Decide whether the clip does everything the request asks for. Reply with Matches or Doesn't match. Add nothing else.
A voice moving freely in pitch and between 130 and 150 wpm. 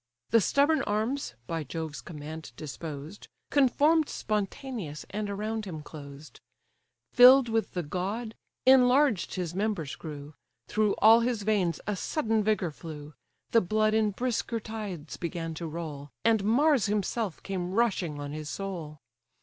Matches